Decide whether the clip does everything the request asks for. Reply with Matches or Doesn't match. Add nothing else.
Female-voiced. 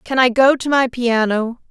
Matches